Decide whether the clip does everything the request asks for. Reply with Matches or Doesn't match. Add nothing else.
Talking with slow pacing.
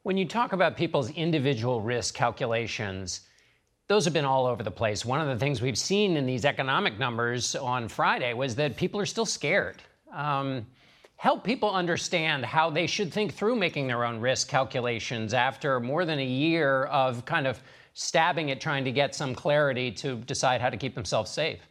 Doesn't match